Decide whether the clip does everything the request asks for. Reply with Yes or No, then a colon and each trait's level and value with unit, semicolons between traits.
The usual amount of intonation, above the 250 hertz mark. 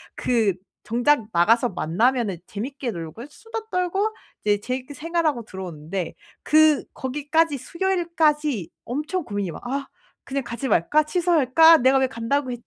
No: wide, 5.7 semitones; very high, 265 Hz